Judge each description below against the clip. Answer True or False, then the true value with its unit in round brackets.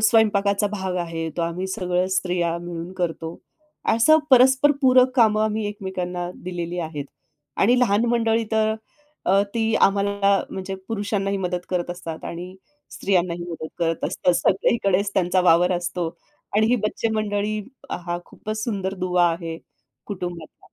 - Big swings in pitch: False (3.4 semitones)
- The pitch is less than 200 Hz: True (190 Hz)